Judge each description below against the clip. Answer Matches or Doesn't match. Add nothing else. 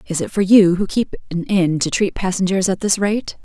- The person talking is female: Matches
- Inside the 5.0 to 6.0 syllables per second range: Matches